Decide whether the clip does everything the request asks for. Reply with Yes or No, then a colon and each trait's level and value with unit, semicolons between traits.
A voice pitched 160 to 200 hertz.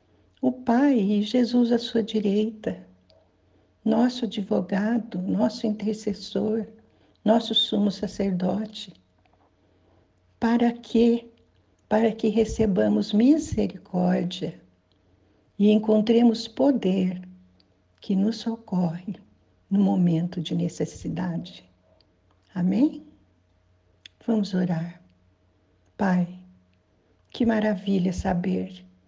Yes: high, 190 Hz